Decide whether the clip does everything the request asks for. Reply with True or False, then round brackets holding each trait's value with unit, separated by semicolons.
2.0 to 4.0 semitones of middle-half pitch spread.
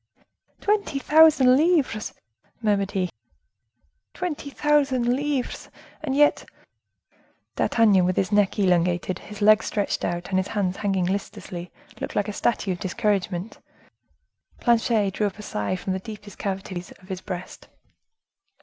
False (5.0 semitones)